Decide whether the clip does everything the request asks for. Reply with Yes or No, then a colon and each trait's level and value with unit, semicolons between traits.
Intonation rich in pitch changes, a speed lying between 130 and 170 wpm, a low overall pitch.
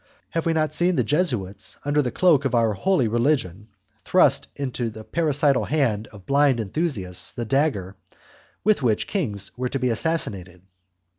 Yes: wide, 6.3 semitones; average, 160 wpm; low, 130 Hz